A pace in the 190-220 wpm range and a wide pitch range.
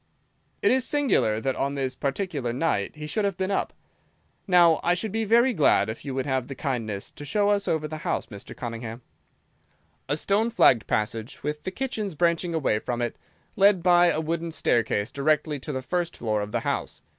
Yes: average, 200 wpm; wide, 7.1 semitones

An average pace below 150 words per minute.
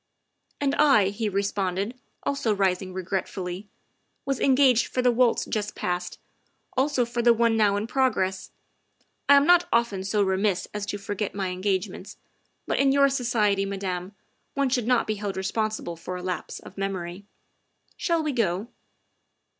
No: average, 170 wpm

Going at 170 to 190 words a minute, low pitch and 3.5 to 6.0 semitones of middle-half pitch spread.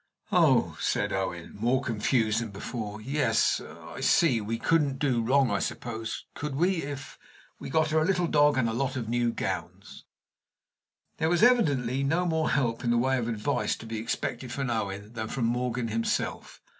Yes: average, 180 wpm; low, 125 Hz; average, 4.1 semitones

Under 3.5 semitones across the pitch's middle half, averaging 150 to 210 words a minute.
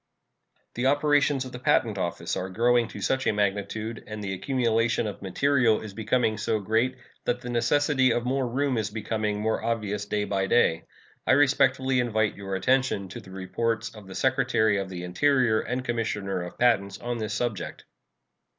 No: average, 3.8 semitones; average, 180 wpm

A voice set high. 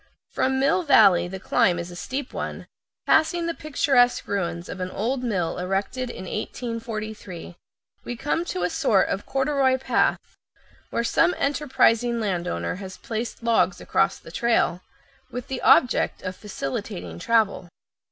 Yes: high, 225 Hz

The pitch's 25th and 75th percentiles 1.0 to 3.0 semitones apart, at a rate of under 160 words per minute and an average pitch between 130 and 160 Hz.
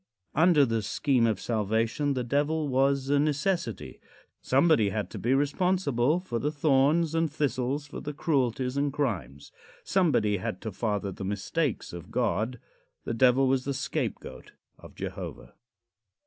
No: average, 4.5 semitones; average, 150 wpm; low, 135 Hz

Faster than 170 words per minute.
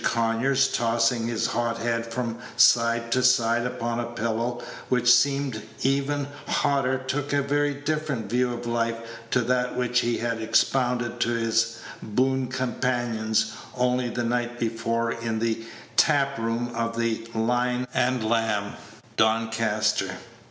No: average, 140 wpm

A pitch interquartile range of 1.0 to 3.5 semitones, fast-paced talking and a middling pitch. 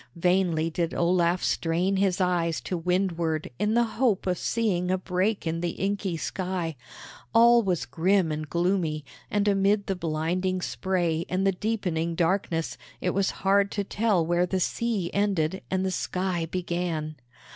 No: average, 2.7 semitones; average, 155 wpm; medium, 180 Hz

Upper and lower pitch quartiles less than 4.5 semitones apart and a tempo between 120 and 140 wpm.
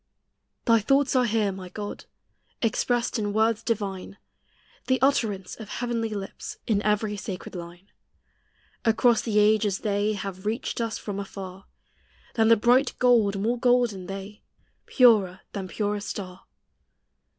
Yes: average, 2.7 semitones; slow, 135 wpm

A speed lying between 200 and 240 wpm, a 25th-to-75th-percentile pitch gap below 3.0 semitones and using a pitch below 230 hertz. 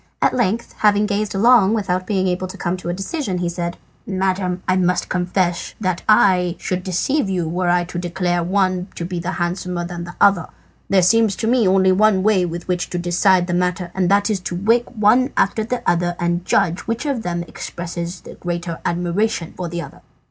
Yes: fast, 205 wpm; narrow, 2.5 semitones; medium, 185 Hz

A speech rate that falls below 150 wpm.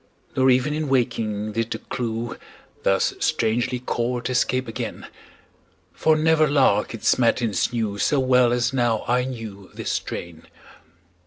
Yes: average, 140 wpm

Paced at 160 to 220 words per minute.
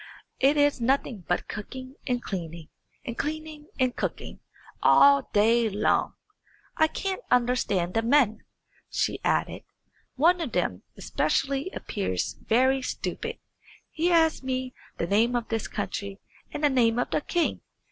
No: average, 140 wpm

